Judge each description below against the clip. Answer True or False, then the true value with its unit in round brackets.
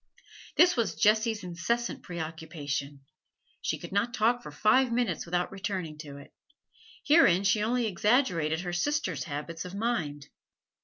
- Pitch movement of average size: False (6.3 semitones)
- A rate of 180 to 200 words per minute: False (140 wpm)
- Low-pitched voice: False (190 Hz)